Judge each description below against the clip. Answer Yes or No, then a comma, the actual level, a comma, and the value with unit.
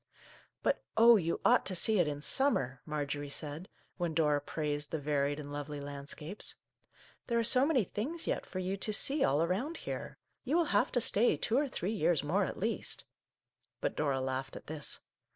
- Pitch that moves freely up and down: Yes, wide, 7.3 semitones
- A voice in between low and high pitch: Yes, medium, 165 Hz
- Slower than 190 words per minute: No, fast, 205 wpm